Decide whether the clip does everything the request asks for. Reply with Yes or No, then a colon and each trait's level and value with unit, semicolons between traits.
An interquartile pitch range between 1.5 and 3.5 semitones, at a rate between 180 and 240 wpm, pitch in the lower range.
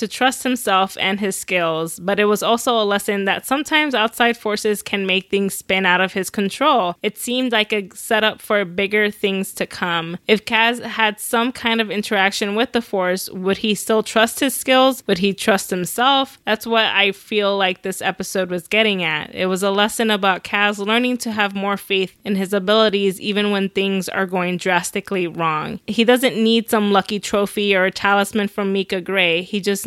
No: narrow, 2.5 semitones; average, 200 wpm; high, 205 Hz